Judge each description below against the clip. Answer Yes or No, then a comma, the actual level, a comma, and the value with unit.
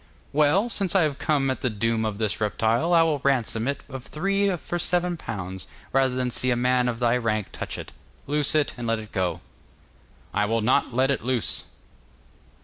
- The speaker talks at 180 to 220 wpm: Yes, average, 200 wpm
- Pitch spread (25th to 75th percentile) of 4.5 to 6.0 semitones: Yes, average, 4.9 semitones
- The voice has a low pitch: Yes, low, 125 Hz